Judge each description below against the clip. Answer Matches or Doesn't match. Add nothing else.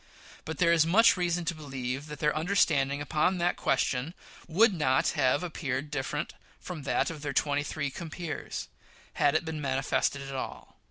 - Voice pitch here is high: Doesn't match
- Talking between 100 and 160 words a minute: Doesn't match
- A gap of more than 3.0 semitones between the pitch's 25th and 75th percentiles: Matches